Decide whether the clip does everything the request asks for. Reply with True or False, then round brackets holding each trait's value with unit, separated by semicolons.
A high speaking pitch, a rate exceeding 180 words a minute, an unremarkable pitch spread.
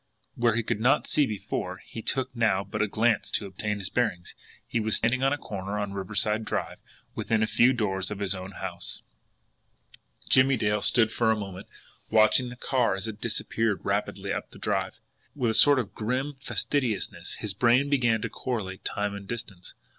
False (110 Hz; 200 wpm; 3.3 semitones)